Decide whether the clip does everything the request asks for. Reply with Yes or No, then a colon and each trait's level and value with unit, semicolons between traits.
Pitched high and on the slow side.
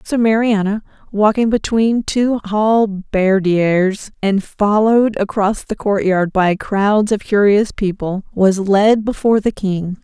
Yes: high, 205 Hz; slow, 125 wpm